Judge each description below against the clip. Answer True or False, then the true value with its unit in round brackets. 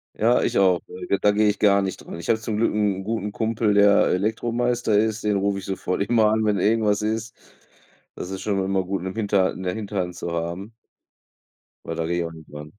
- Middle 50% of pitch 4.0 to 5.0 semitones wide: False (2.7 semitones)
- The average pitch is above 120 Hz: False (100 Hz)